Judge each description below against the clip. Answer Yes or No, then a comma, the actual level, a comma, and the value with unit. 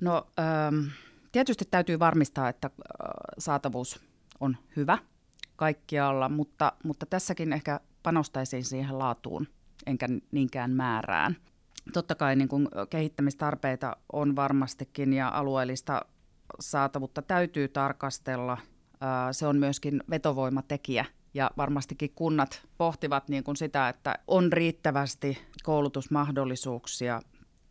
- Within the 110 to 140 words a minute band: No, slow, 95 wpm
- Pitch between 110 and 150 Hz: Yes, medium, 140 Hz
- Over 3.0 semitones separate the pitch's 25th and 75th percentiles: No, narrow, 2.5 semitones